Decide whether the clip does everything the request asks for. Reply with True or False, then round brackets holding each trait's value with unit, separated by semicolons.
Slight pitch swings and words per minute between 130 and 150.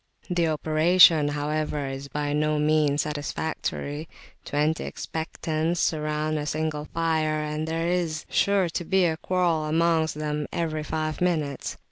True (1.5 semitones; 135 wpm)